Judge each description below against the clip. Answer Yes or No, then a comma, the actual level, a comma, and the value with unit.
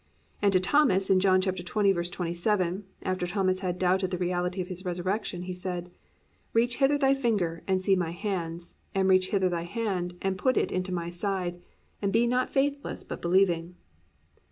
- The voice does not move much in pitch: Yes, narrow, 2.2 semitones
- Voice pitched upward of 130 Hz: Yes, medium, 185 Hz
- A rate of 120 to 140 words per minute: No, average, 175 wpm